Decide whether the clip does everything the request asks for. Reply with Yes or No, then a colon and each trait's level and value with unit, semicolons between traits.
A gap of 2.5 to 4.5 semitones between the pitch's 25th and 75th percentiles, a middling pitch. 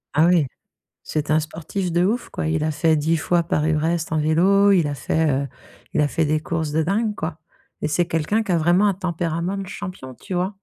Yes: average, 2.8 semitones; medium, 165 Hz